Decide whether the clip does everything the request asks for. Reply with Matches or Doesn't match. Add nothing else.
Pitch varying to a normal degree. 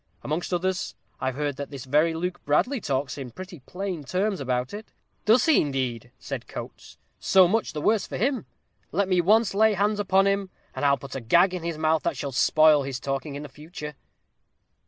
Doesn't match